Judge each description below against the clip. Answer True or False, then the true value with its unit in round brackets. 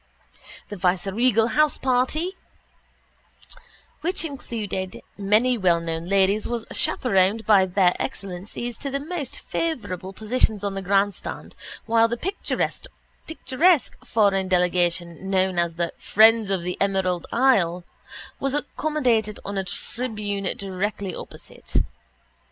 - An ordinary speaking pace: False (110 wpm)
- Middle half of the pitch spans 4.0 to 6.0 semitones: True (4.6 semitones)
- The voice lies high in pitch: True (205 Hz)